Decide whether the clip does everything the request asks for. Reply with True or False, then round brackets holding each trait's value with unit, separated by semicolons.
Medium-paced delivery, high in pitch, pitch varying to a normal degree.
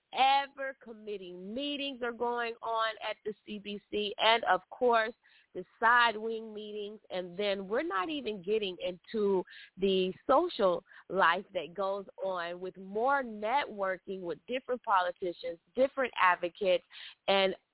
False (130 wpm; 205 Hz; 4.0 semitones)